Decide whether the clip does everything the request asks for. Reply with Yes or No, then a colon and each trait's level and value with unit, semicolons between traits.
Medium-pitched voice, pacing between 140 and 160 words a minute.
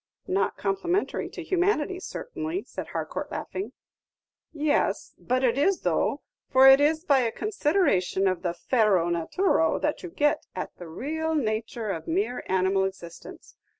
No: very high, 265 Hz; average, 150 wpm